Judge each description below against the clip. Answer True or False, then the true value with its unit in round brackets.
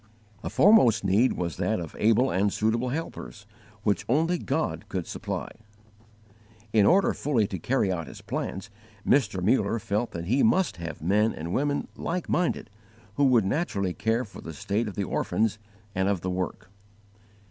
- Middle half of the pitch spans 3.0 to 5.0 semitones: False (5.4 semitones)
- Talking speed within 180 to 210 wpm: False (170 wpm)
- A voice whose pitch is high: False (105 Hz)